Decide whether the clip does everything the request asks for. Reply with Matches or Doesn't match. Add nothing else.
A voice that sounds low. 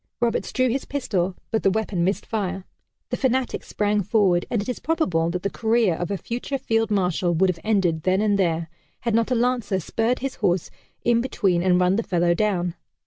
Doesn't match